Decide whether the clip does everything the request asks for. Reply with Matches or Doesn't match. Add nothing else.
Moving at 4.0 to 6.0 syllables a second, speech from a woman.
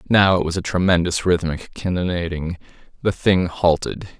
Doesn't match